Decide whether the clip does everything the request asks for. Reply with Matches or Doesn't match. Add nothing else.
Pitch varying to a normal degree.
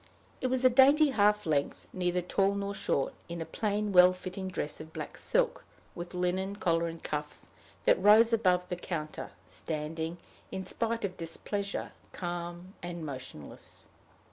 Matches